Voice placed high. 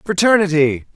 No: medium, 170 Hz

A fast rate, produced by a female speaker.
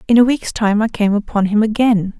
Yes: fast, 245 wpm; female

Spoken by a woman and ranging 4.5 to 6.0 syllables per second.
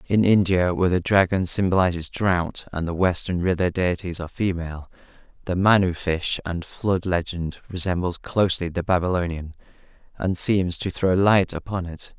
No: male; 5.0 syllables/s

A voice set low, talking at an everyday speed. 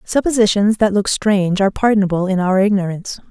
No: high, 200 Hz; average, 165 wpm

